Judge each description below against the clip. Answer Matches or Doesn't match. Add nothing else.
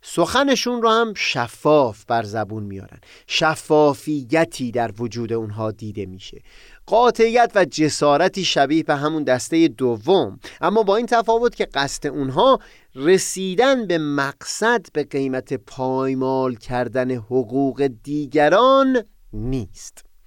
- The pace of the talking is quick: Doesn't match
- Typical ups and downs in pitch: Doesn't match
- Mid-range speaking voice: Matches